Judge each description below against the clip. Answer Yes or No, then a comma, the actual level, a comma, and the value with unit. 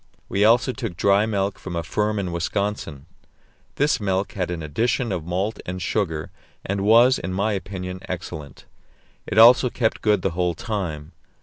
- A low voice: Yes, very low, 95 Hz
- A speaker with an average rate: Yes, average, 170 wpm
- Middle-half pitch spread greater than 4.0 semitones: No, average, 3.5 semitones